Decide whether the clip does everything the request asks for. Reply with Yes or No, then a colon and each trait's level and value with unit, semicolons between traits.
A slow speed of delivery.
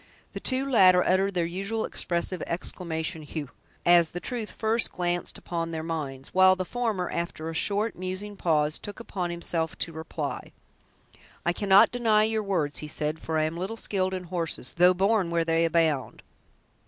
No: average, 175 wpm